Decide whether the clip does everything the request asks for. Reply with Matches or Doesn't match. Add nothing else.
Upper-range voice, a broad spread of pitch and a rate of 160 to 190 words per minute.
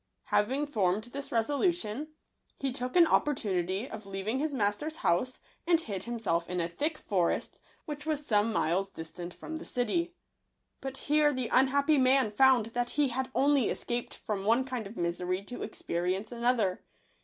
Matches